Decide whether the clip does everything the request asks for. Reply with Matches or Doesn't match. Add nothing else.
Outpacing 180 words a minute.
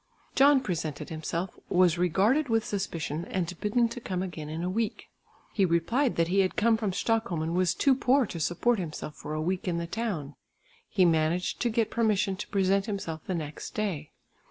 Matches